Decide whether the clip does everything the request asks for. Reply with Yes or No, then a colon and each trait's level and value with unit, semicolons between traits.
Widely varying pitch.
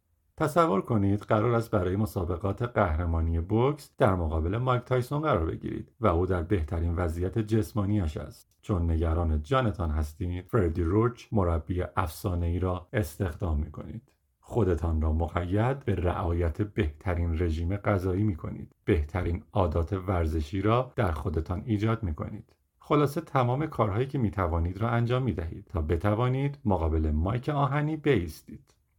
No: average, 4.9 semitones